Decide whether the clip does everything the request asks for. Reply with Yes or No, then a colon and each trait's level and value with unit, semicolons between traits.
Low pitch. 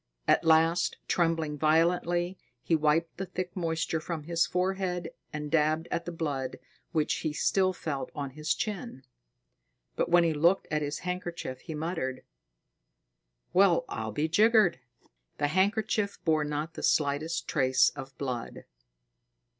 No: medium, 165 Hz